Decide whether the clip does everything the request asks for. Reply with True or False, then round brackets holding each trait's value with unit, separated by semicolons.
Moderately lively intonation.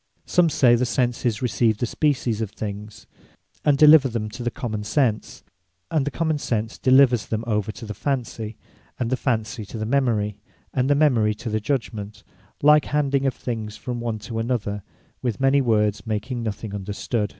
True (3.8 semitones)